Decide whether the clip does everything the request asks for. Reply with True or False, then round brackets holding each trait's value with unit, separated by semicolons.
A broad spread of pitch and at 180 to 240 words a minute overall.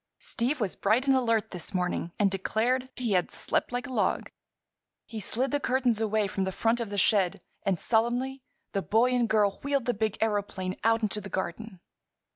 False (3.8 semitones; 195 wpm)